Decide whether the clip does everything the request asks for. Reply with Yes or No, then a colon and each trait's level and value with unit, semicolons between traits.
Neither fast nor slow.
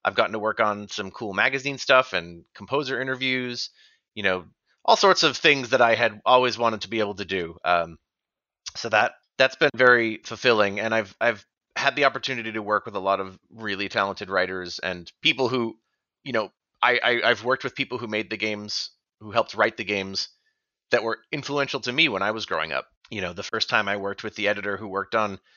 No: fast, 220 wpm